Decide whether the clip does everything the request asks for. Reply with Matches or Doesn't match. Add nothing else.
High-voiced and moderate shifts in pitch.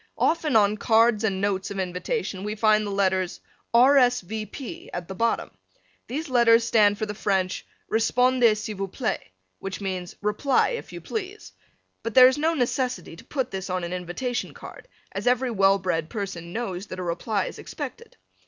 Matches